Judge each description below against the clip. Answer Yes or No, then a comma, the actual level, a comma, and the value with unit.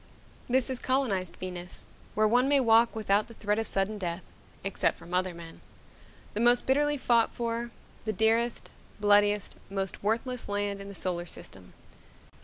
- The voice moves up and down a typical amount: Yes, average, 3.6 semitones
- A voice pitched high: Yes, high, 210 Hz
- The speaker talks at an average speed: Yes, average, 160 wpm